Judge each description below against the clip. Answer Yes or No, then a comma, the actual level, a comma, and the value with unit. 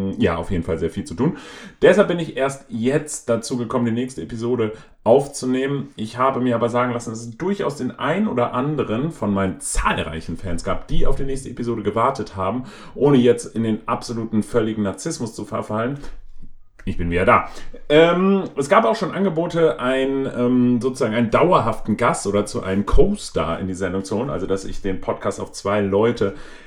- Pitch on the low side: Yes, low, 120 Hz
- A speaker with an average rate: No, fast, 195 wpm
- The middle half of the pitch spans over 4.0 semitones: Yes, wide, 5.4 semitones